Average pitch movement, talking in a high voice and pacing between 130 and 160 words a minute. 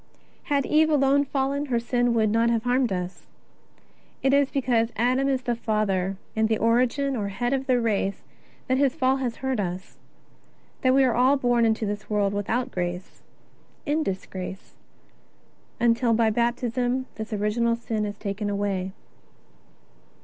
Yes: average, 3.8 semitones; high, 235 Hz; average, 155 wpm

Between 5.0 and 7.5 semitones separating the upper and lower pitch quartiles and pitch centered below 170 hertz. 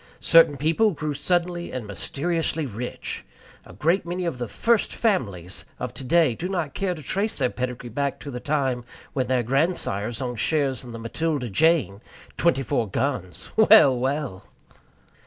Yes: wide, 5.6 semitones; medium, 140 Hz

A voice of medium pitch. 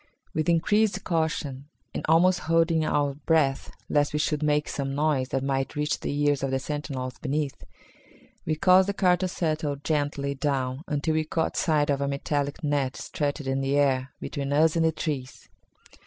Yes: medium, 145 Hz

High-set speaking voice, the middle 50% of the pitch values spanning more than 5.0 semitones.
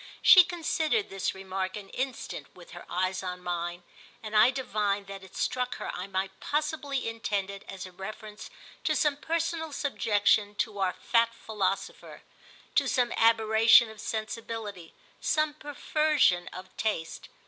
Yes: high, 215 Hz; wide, 5.6 semitones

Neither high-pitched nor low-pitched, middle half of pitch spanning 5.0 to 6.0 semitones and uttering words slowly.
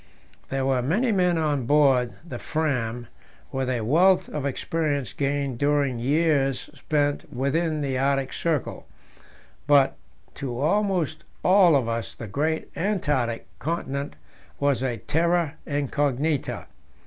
No: medium, 145 Hz; average, 3.3 semitones; slow, 125 wpm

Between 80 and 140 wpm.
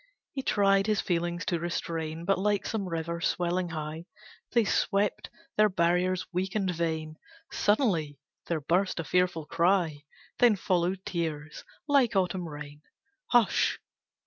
Yes: slow, 135 wpm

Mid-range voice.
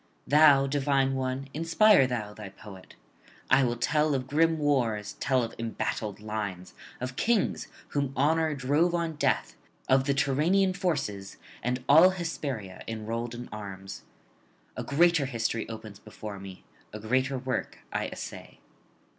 No: low, 130 Hz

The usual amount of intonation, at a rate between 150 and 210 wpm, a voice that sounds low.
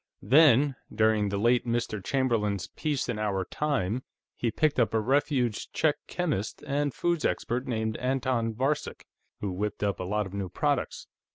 Yes: average, 4.6 semitones; average, 165 wpm; low, 120 Hz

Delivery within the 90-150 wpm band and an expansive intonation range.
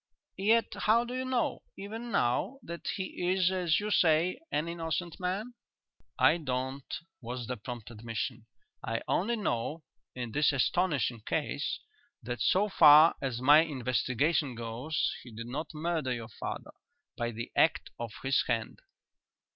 Yes: average, 145 wpm; wide, 7.0 semitones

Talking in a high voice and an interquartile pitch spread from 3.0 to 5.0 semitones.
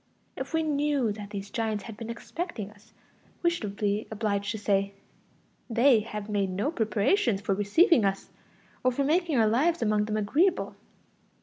No: high, 220 Hz; wide, 5.5 semitones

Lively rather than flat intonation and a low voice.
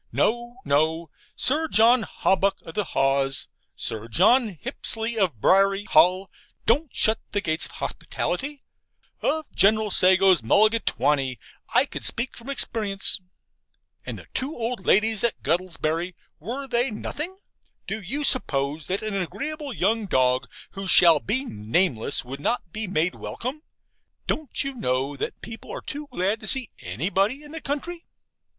No: wide, 6.8 semitones; high, 200 Hz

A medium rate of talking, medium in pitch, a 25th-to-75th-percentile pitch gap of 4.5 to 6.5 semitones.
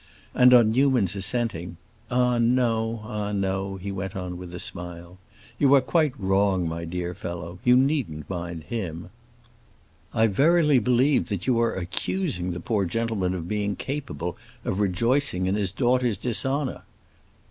No: average, 150 wpm; low, 105 Hz; wide, 5.5 semitones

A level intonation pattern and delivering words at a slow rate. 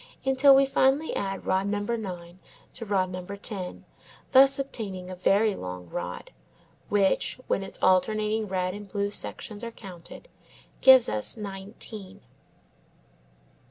No: average, 3.5 semitones; slow, 130 wpm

